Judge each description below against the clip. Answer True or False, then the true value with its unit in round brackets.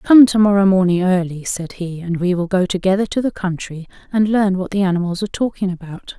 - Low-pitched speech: False (190 Hz)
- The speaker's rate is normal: False (225 wpm)